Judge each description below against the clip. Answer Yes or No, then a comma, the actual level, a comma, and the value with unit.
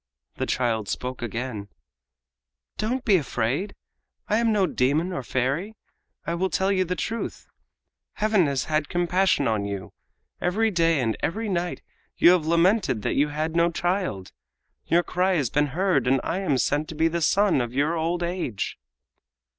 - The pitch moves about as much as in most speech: No, wide, 6.0 semitones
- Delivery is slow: No, average, 170 wpm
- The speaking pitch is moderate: Yes, medium, 165 Hz